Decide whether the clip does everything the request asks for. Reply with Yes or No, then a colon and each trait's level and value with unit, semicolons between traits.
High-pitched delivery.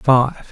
No: low, 135 Hz